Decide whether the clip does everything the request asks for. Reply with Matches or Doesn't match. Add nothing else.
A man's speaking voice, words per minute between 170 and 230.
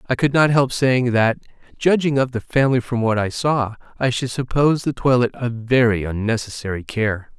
Matches